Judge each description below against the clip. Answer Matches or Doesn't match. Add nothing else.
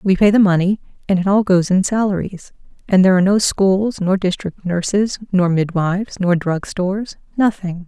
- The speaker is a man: Doesn't match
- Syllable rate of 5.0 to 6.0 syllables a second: Matches